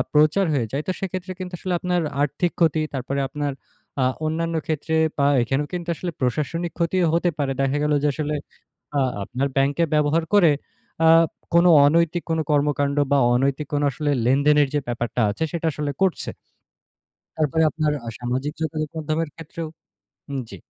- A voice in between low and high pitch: Yes, medium, 150 Hz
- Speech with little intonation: No, average, 3.0 semitones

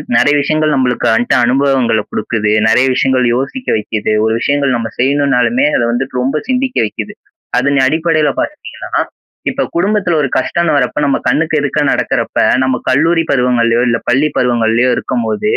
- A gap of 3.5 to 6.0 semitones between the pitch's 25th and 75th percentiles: Yes, average, 3.9 semitones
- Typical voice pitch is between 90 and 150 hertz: Yes, low, 135 Hz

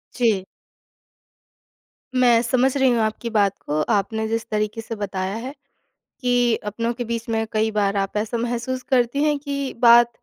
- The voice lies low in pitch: No, high, 230 Hz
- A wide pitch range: No, narrow, 2.5 semitones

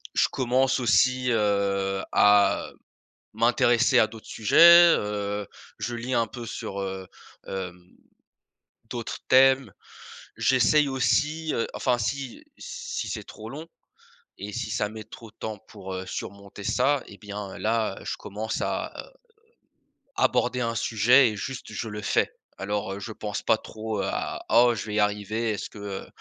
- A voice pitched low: Yes, low, 110 Hz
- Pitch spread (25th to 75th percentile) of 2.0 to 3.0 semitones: No, average, 3.5 semitones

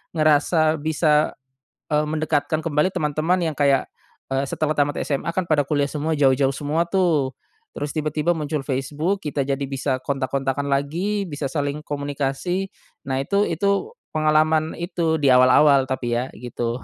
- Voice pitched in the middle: Yes, medium, 150 Hz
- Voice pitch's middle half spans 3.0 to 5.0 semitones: No, narrow, 2.4 semitones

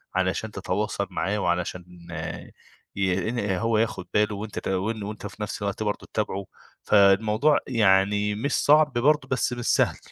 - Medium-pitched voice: No, low, 105 Hz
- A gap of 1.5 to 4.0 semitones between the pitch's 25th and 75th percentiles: Yes, narrow, 2.5 semitones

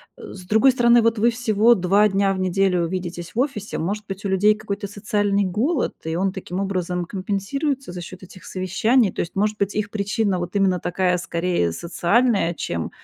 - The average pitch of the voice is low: No, high, 195 Hz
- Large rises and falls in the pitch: No, average, 2.9 semitones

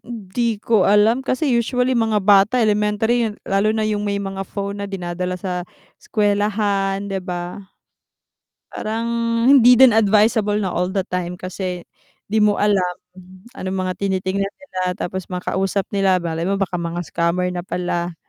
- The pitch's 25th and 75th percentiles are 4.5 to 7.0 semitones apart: No, average, 2.8 semitones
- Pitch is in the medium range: No, high, 200 Hz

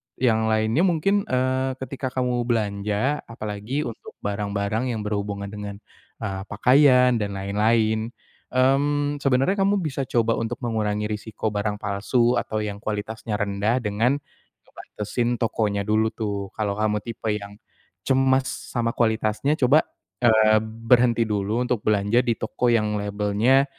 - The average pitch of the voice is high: No, low, 110 Hz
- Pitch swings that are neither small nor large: Yes, average, 3.4 semitones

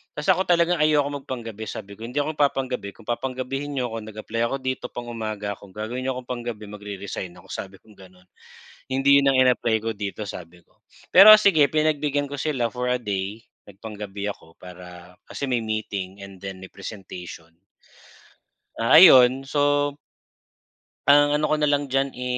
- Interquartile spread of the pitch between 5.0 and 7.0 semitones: Yes, wide, 5.6 semitones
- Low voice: Yes, low, 120 Hz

